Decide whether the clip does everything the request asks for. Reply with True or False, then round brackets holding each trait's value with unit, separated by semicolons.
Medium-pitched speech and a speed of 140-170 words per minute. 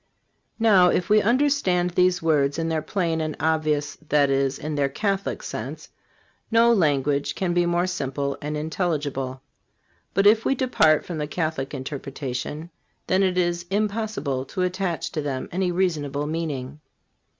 True (160 Hz; 150 wpm)